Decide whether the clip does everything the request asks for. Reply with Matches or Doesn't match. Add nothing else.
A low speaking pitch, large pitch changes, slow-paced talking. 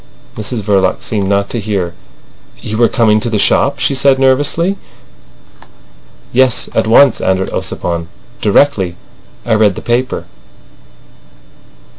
Doesn't match